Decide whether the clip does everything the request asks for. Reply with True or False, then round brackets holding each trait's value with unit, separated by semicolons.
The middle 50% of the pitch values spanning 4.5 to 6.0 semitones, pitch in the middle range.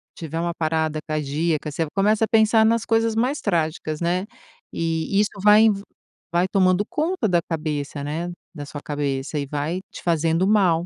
True (5.0 semitones; 170 Hz)